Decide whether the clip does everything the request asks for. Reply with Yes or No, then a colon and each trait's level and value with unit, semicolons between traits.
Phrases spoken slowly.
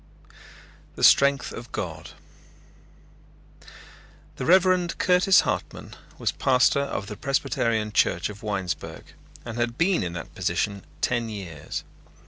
Yes: slow, 115 wpm